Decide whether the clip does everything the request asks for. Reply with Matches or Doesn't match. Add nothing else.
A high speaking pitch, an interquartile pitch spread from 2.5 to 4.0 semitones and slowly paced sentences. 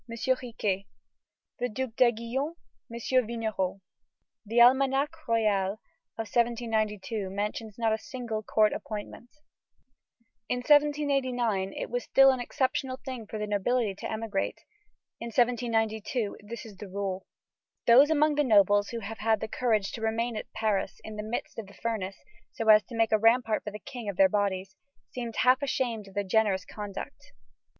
Doesn't match